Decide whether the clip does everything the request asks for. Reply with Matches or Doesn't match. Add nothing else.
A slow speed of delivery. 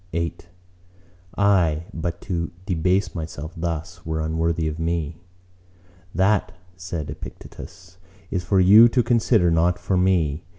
Matches